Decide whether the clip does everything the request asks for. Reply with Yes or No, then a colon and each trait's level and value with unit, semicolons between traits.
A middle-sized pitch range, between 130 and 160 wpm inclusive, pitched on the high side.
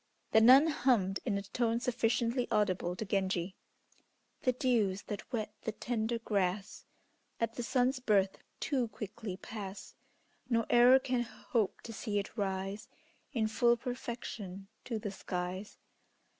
Yes: average, 3.6 semitones; average, 140 wpm; high, 220 Hz